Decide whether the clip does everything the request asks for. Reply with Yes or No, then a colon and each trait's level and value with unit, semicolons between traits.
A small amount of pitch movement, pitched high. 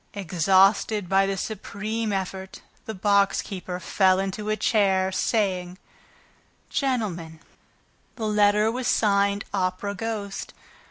Yes: narrow, 2.1 semitones; high, 200 Hz